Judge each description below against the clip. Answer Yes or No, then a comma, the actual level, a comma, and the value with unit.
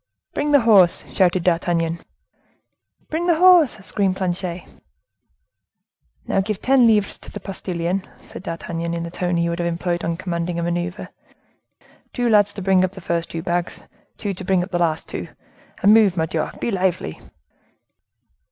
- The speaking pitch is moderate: Yes, medium, 180 Hz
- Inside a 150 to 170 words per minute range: Yes, average, 160 wpm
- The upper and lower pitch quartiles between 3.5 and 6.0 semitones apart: No, average, 3.1 semitones